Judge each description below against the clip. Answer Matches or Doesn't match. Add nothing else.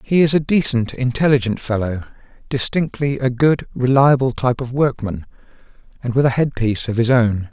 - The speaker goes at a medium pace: Matches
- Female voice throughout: Doesn't match